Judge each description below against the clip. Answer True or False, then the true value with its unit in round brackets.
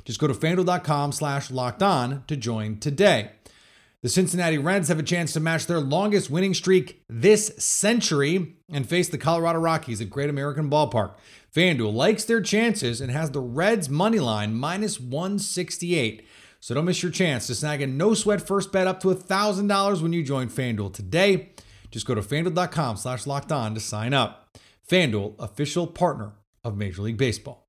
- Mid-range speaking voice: True (155 Hz)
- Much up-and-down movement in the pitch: True (6.9 semitones)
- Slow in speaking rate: False (180 wpm)